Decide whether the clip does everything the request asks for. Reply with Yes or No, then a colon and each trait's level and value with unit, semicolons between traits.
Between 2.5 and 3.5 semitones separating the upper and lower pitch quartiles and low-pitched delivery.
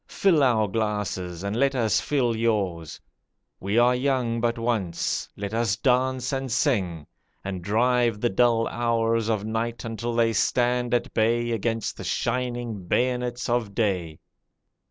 Yes: average, 2.9 semitones; low, 115 Hz